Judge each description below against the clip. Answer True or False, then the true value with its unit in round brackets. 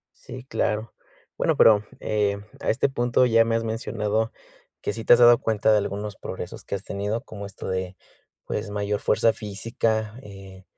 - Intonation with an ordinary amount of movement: False (2.0 semitones)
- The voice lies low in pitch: True (105 Hz)